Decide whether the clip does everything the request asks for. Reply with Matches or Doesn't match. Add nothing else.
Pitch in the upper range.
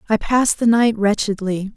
Matches